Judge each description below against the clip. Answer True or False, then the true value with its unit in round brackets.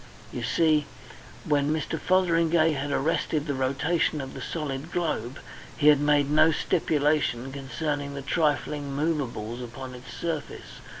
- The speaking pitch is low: False (145 Hz)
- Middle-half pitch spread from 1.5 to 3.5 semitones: True (2.6 semitones)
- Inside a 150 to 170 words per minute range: False (135 wpm)